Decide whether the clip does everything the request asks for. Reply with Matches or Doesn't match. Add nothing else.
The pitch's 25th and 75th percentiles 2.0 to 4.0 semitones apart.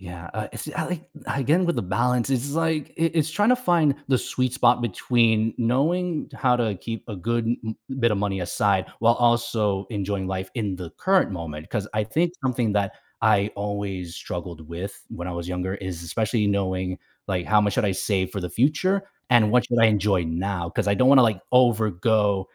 Doesn't match